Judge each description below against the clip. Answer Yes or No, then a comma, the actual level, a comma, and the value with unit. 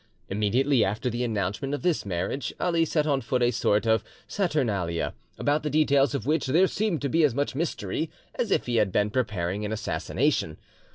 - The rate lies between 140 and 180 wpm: No, average, 190 wpm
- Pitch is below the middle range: Yes, low, 130 Hz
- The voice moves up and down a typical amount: No, wide, 6.1 semitones